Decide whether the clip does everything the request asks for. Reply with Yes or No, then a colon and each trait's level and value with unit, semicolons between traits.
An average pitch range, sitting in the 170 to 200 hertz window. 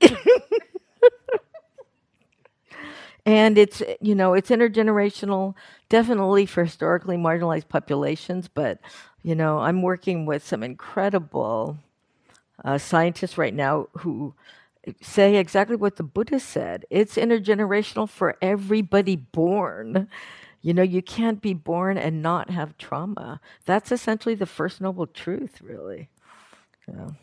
Yes: average, 4.1 semitones; high, 190 Hz